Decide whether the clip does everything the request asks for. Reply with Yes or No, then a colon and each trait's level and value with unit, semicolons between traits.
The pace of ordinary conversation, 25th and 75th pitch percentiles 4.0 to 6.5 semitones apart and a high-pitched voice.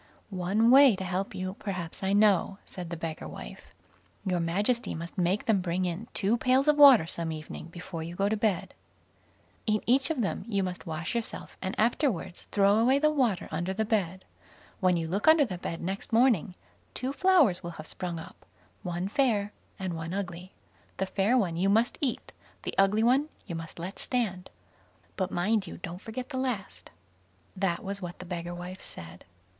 Yes: average, 190 wpm; average, 4.4 semitones; high, 195 Hz